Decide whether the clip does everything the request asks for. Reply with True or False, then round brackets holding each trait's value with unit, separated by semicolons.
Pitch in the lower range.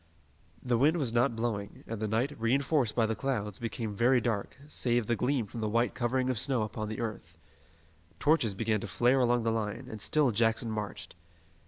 True (115 Hz)